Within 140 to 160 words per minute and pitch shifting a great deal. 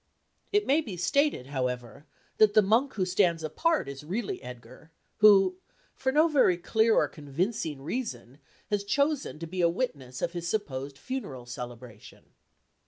Yes: average, 155 wpm; wide, 8.7 semitones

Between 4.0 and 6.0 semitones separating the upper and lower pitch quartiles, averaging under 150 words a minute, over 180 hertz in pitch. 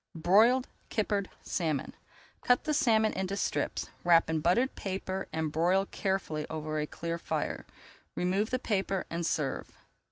Yes: average, 4.5 semitones; average, 140 wpm; high, 190 Hz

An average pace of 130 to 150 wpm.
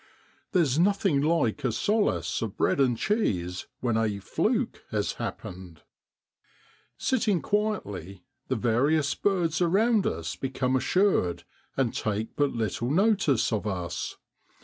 Yes: average, 145 wpm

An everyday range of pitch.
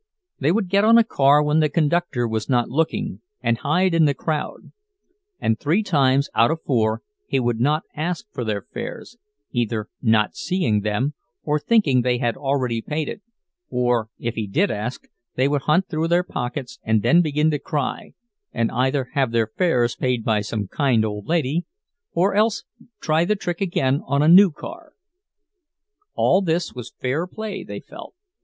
No: wide, 6.2 semitones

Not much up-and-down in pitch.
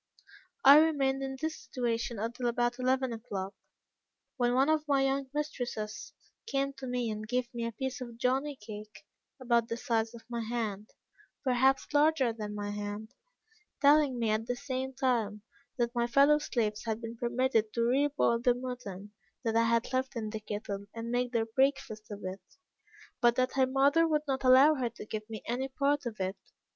No: average, 3.2 semitones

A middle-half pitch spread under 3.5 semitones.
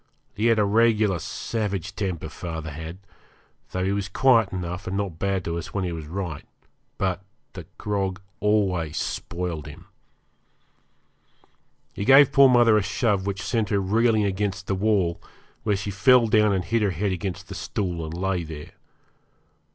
Yes: average, 2.9 semitones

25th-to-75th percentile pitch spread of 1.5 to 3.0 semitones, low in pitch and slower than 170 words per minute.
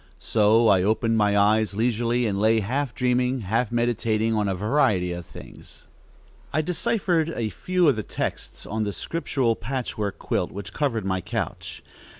No: average, 3.4 semitones; low, 115 Hz; average, 160 wpm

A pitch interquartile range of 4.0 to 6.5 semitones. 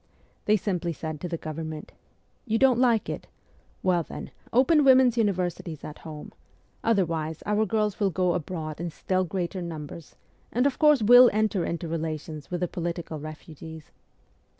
Yes: average, 5.2 semitones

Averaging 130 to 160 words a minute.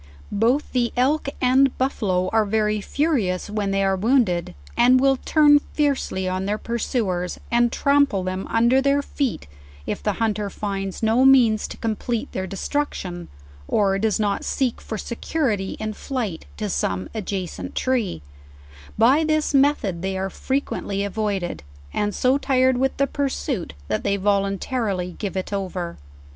Yes: average, 155 wpm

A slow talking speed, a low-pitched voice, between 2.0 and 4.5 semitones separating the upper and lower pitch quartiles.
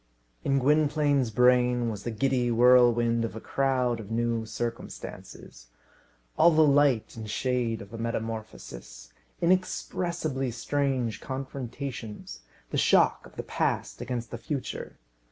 Yes: slow, 125 wpm; low, 120 Hz; average, 3.2 semitones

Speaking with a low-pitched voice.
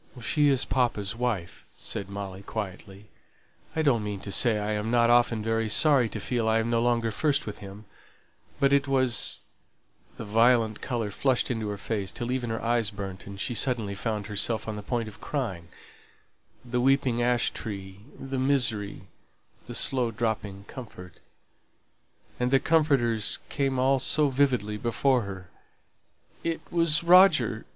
Yes: low, 115 Hz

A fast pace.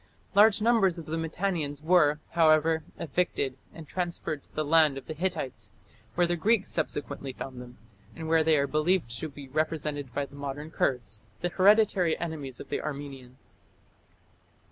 No: average, 165 wpm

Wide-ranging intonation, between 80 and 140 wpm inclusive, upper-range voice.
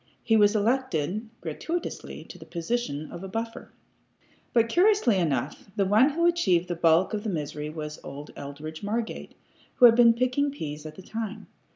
No: wide, 7.0 semitones; average, 175 wpm; high, 200 Hz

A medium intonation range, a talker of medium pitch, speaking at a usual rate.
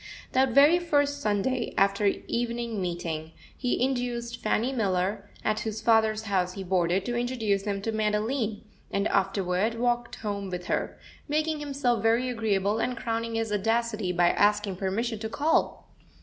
No: average, 3.4 semitones; high, 220 Hz; average, 150 wpm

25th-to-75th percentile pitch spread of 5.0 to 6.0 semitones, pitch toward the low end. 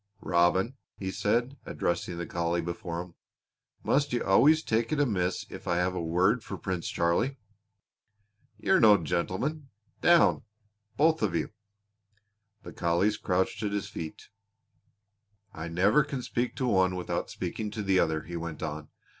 Yes: wide, 5.4 semitones; very low, 95 Hz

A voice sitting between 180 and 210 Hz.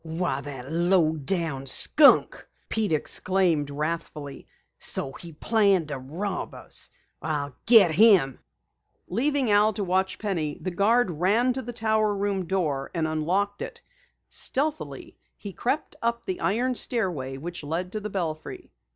Yes: medium, 185 Hz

